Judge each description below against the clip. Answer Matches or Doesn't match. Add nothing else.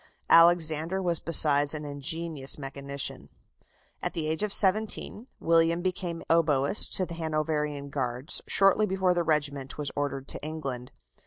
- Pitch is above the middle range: Doesn't match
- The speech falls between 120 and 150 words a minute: Matches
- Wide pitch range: Doesn't match